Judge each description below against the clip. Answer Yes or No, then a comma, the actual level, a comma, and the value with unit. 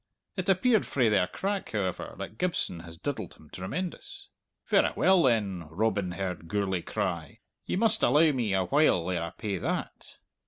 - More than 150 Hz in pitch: No, low, 105 Hz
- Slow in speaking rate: No, average, 165 wpm